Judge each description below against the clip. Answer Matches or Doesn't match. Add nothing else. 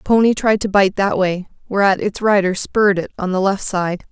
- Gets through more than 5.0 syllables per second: Matches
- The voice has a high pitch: Matches